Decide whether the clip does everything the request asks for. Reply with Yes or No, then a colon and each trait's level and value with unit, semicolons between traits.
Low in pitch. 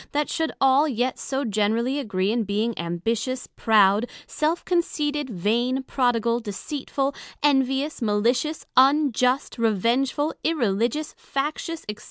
No: very high, 255 Hz